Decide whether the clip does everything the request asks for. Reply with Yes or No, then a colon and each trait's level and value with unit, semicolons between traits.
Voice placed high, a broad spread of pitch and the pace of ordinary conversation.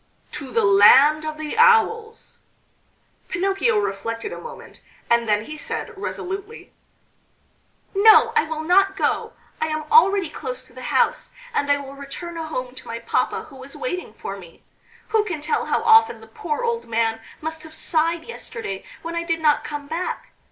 Yes: very high, 315 Hz; wide, 6.8 semitones; average, 175 wpm